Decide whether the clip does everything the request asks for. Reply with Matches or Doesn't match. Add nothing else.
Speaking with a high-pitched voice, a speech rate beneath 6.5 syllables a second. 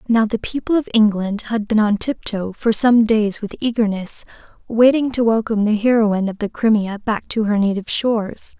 Matches